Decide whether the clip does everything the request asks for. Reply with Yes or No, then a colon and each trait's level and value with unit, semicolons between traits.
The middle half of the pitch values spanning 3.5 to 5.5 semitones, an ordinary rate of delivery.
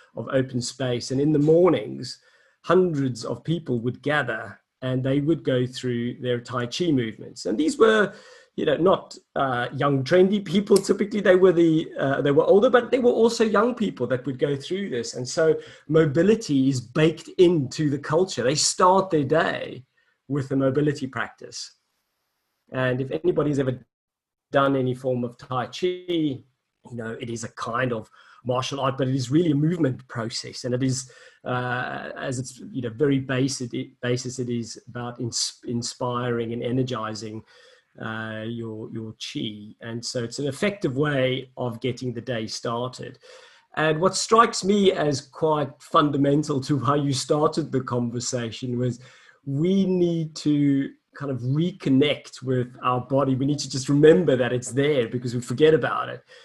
Yes: average, 4.4 semitones; average, 170 wpm